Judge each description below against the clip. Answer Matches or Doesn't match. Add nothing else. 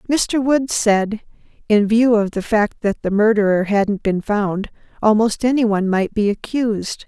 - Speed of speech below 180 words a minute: Matches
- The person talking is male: Doesn't match